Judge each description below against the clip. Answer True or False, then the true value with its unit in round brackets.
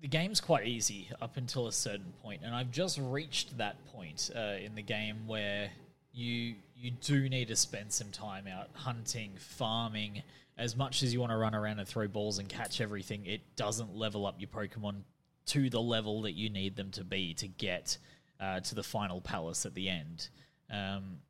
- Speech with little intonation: False (4.0 semitones)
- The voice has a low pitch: True (110 Hz)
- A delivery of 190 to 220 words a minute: True (200 wpm)